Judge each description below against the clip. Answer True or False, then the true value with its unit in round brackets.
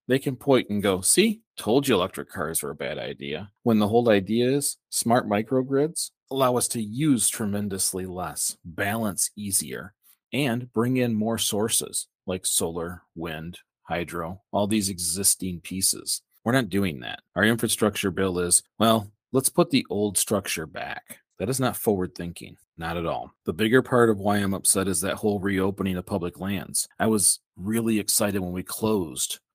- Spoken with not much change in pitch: False (3.7 semitones)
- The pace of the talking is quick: False (175 wpm)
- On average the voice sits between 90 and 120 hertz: True (105 Hz)